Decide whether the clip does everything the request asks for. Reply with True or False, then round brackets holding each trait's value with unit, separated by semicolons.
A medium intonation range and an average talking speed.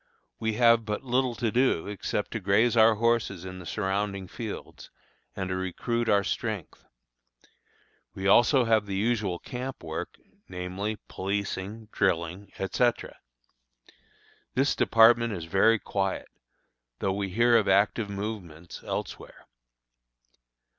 False (3.4 semitones; 125 wpm)